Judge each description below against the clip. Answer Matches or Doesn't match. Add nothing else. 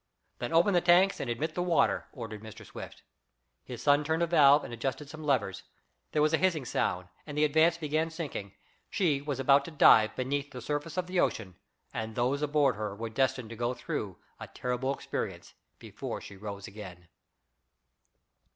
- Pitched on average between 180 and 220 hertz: Doesn't match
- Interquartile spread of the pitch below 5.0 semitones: Doesn't match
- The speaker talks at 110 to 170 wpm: Doesn't match